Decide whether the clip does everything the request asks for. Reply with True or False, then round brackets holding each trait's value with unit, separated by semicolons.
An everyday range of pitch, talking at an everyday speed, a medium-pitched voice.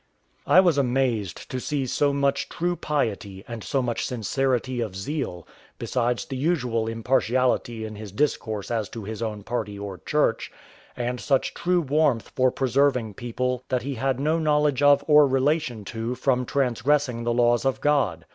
False (3.8 semitones; 165 wpm; 125 Hz)